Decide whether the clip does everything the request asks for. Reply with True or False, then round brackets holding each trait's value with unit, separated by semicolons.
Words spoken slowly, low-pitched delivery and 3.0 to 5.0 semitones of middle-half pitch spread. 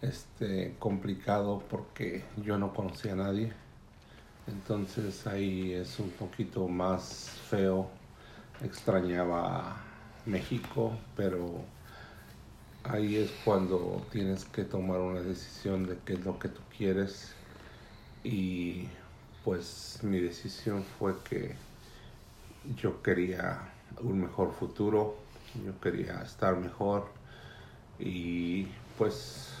False (105 wpm; 95 Hz; 2.5 semitones)